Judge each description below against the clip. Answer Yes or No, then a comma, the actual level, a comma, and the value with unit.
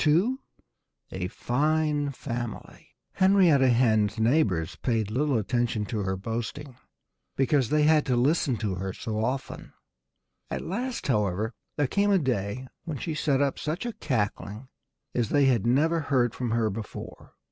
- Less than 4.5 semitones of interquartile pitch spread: No, average, 5.3 semitones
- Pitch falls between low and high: No, low, 125 Hz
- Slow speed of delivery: No, average, 150 wpm